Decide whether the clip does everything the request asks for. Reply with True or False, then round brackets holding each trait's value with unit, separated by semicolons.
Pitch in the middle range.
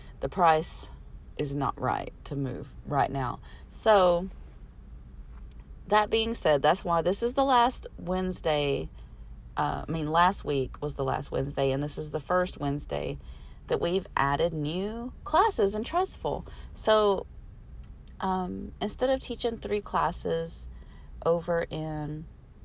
True (155 Hz)